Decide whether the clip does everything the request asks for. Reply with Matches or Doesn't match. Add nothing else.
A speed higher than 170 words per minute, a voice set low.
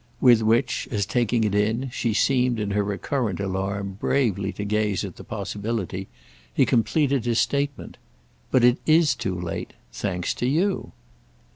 Doesn't match